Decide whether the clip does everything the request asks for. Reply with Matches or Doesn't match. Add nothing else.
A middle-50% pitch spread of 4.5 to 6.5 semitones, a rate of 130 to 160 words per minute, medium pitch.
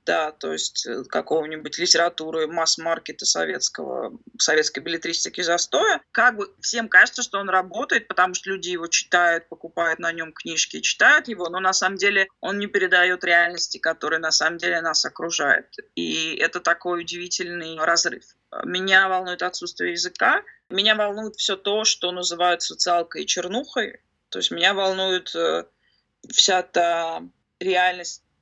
Doesn't match